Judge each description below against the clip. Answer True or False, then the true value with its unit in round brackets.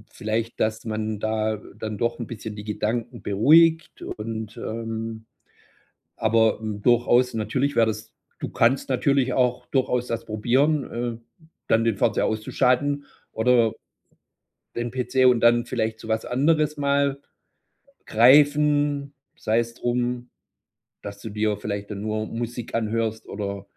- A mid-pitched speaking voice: False (115 Hz)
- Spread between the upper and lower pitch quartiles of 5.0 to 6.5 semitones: False (2.7 semitones)